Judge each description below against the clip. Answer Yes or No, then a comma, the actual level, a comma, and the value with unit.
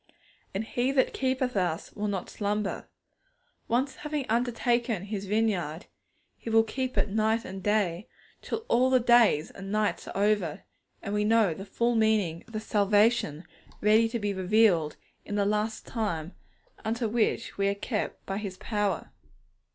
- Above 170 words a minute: No, average, 160 wpm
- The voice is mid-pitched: No, high, 215 Hz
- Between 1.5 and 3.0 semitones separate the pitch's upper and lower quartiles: Yes, average, 2.7 semitones